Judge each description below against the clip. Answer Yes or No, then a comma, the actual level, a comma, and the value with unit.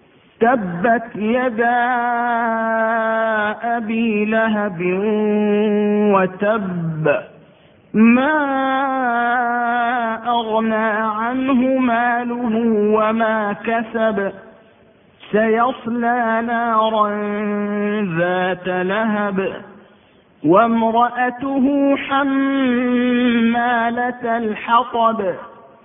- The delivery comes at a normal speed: No, slow, 40 wpm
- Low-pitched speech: No, high, 230 Hz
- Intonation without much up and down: Yes, narrow, 2.3 semitones